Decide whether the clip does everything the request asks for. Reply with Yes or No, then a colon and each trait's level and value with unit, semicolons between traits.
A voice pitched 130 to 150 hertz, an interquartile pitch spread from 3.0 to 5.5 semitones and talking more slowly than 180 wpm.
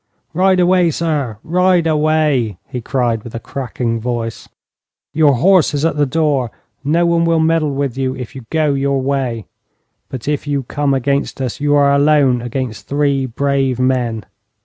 Yes: medium, 140 Hz; average, 3.5 semitones; average, 170 wpm